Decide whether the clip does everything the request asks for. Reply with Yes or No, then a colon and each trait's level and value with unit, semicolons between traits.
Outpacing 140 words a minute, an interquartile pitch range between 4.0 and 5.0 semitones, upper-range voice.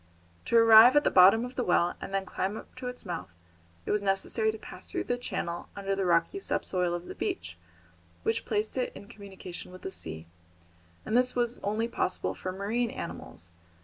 Yes: fast, 205 wpm; average, 4.3 semitones; high, 200 Hz